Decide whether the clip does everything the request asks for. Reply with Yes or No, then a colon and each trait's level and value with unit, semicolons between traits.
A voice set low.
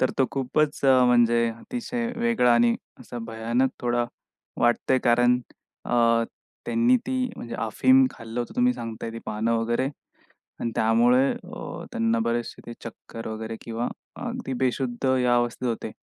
Yes: low, 120 Hz